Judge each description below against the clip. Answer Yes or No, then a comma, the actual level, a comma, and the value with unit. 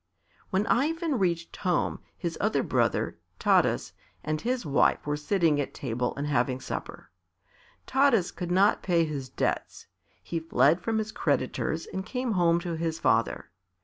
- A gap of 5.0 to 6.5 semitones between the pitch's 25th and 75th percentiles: Yes, wide, 5.5 semitones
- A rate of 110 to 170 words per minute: Yes, average, 150 wpm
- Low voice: No, medium, 170 Hz